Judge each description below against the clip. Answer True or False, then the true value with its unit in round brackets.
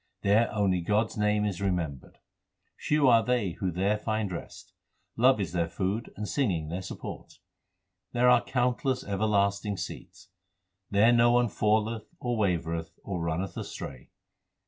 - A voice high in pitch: False (105 Hz)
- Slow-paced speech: False (145 wpm)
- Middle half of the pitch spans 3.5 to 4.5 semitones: True (4.0 semitones)